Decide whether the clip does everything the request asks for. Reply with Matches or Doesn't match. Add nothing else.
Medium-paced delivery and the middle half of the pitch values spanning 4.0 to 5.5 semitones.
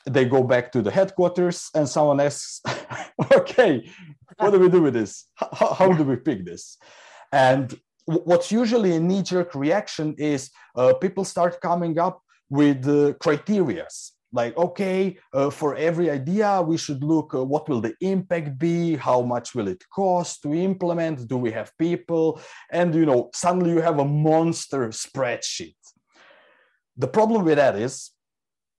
Matches